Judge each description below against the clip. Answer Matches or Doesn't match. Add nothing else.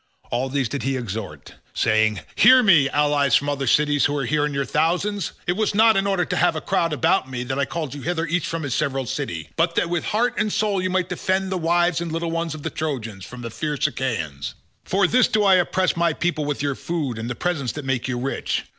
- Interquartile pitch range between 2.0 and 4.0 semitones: Doesn't match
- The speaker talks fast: Matches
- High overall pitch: Doesn't match